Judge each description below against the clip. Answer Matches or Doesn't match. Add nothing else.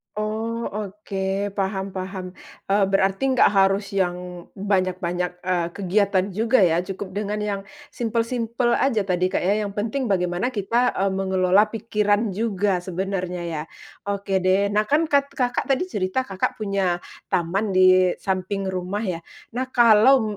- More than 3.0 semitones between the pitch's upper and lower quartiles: Doesn't match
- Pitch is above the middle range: Matches